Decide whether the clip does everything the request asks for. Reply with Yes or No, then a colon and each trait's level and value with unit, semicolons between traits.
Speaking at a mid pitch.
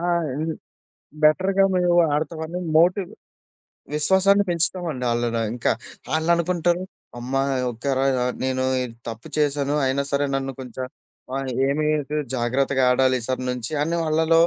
Yes: medium, 145 Hz